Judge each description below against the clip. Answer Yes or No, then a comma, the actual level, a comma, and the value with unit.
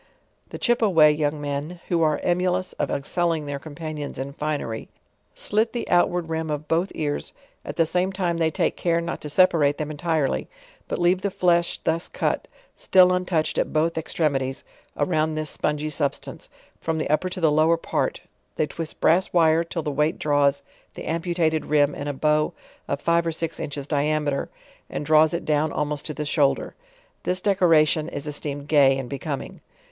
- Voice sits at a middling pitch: Yes, medium, 155 Hz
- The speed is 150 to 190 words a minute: Yes, average, 185 wpm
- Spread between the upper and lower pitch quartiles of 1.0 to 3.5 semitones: Yes, narrow, 2.6 semitones